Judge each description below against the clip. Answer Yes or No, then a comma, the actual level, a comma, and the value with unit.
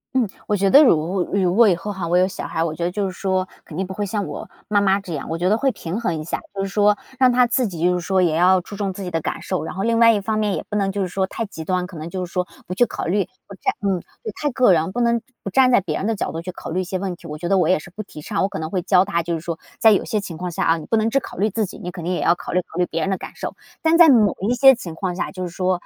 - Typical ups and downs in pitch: Yes, average, 3.1 semitones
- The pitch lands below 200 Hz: Yes, high, 190 Hz